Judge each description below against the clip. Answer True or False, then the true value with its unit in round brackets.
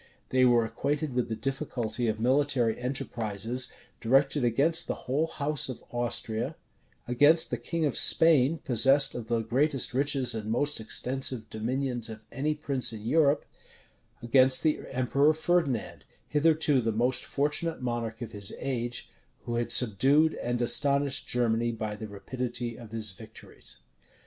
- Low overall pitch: True (125 Hz)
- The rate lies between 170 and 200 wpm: False (145 wpm)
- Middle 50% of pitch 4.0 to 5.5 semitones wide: False (3.5 semitones)